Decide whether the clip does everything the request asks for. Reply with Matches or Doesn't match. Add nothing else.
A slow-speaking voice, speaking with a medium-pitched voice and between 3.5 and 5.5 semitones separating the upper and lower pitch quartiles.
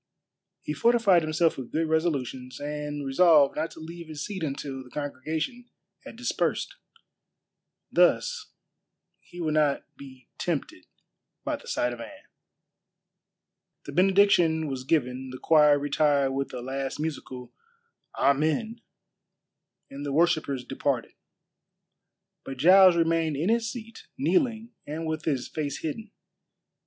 Matches